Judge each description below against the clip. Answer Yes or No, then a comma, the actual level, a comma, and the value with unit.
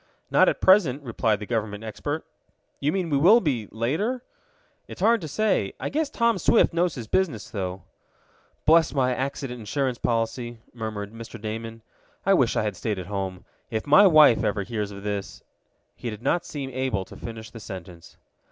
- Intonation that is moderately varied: No, wide, 6.4 semitones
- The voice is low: Yes, low, 120 Hz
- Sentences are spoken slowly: No, average, 180 wpm